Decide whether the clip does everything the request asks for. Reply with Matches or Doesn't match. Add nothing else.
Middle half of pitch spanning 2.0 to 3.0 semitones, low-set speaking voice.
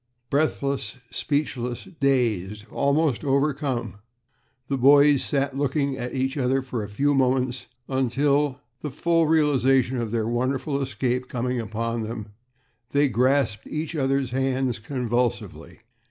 Matches